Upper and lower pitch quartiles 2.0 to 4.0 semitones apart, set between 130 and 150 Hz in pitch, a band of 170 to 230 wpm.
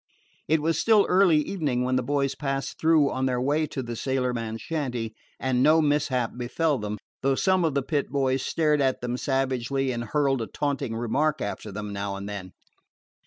Yes: average, 3.6 semitones; low, 135 Hz; average, 190 wpm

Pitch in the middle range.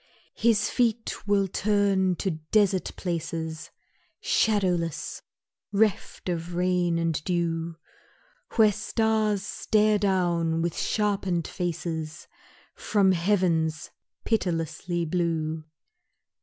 Yes: medium, 180 Hz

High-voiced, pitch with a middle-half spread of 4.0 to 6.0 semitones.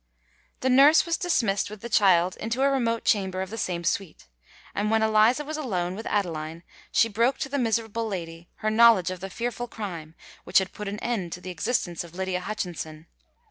Yes: high, 205 Hz; average, 4.4 semitones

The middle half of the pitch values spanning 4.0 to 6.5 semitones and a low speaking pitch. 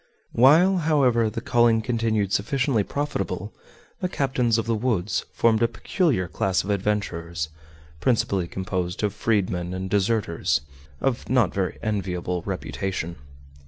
Yes: average, 4.4 semitones; low, 105 Hz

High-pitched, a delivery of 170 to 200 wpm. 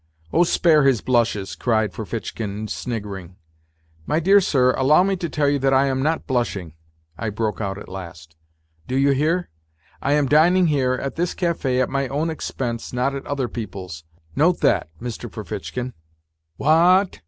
No: low, 130 Hz; average, 175 wpm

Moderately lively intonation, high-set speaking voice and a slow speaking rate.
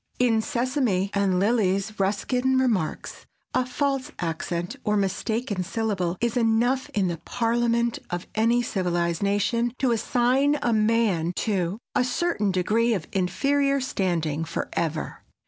Yes: average, 4.7 semitones; high, 220 Hz; slow, 130 wpm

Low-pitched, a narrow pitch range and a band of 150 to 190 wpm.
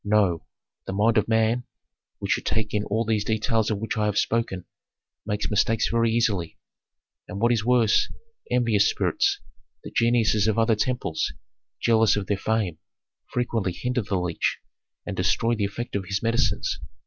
Yes: low, 110 Hz; narrow, 2.2 semitones; average, 165 wpm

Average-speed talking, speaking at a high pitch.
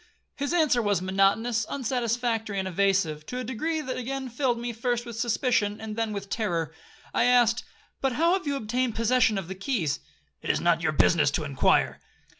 Yes: average, 185 wpm; high, 225 Hz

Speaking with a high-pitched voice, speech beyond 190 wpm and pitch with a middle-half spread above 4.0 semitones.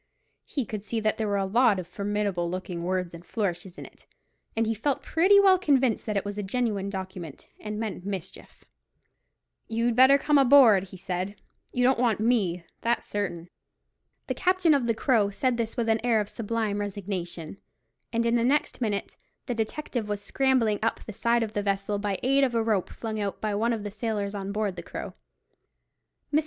No: high, 215 Hz; average, 200 wpm; average, 3.2 semitones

